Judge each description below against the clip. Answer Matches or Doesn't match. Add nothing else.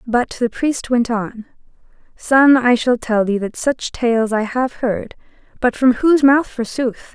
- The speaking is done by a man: Doesn't match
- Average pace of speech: Matches